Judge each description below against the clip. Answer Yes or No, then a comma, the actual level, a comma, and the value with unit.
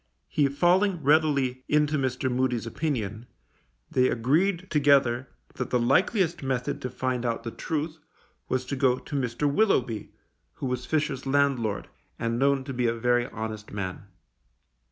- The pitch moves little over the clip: No, average, 3.5 semitones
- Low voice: Yes, low, 130 Hz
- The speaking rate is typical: Yes, average, 150 wpm